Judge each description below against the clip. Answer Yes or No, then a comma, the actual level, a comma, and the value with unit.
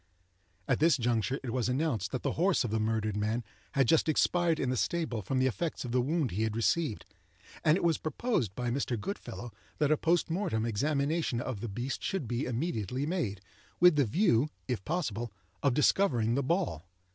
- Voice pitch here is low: Yes, low, 130 Hz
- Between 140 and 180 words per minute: No, average, 195 wpm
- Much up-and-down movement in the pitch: Yes, wide, 6.0 semitones